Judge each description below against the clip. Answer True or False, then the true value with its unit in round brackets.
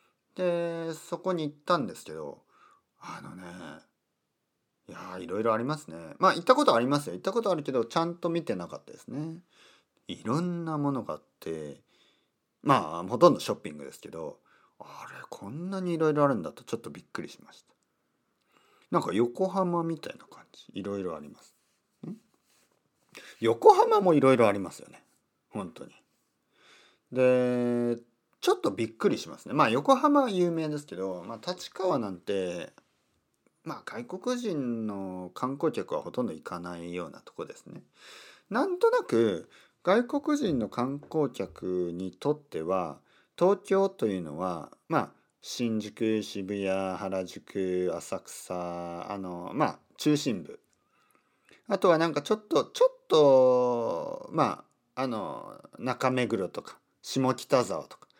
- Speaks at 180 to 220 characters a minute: False (285 characters per minute)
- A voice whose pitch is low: False (145 Hz)